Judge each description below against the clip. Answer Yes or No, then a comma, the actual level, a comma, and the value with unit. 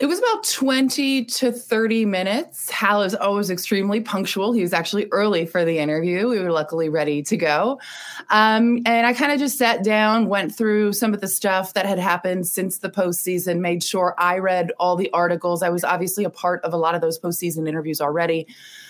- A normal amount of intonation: Yes, average, 4.3 semitones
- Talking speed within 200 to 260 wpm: Yes, fast, 205 wpm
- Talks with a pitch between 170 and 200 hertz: Yes, high, 190 Hz